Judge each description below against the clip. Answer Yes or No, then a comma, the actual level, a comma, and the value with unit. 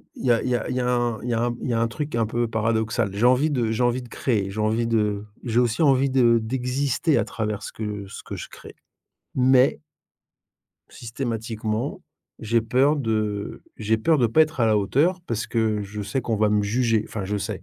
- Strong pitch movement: No, average, 2.7 semitones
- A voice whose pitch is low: Yes, low, 115 Hz